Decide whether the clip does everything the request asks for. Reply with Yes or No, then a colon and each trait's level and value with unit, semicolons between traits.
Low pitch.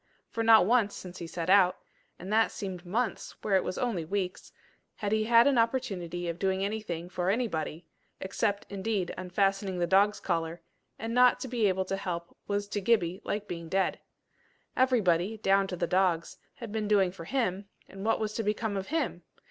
No: high, 195 Hz